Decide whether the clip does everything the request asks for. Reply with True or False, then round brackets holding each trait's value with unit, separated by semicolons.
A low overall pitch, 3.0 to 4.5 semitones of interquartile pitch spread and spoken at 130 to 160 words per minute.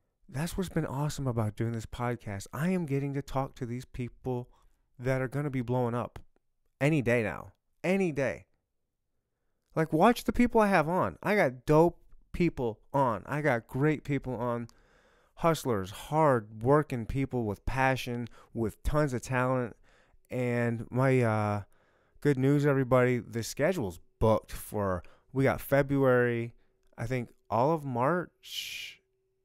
True (130 Hz; 3.8 semitones; 150 wpm)